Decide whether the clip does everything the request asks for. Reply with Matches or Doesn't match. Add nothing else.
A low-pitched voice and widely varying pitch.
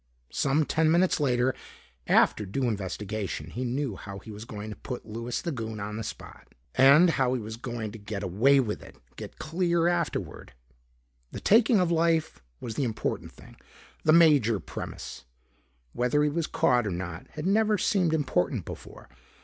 Matches